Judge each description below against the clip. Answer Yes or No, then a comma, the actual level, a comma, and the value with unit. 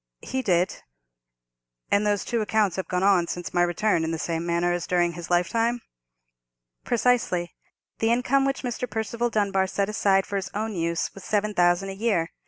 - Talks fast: No, average, 185 wpm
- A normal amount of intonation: Yes, average, 4.0 semitones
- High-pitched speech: Yes, high, 195 Hz